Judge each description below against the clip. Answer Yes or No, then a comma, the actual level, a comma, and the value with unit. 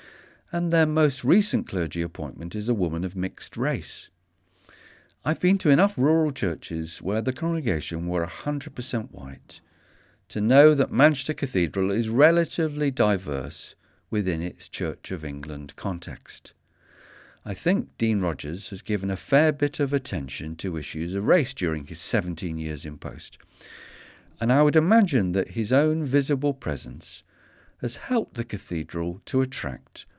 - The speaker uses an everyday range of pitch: No, wide, 9.0 semitones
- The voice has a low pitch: Yes, low, 100 Hz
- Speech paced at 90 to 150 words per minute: Yes, average, 145 wpm